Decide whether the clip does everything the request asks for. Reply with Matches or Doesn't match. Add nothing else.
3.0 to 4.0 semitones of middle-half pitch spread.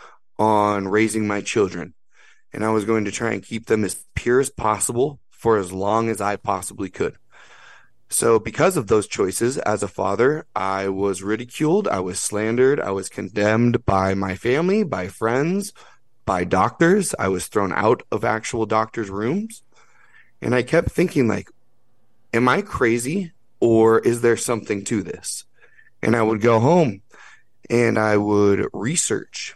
Matches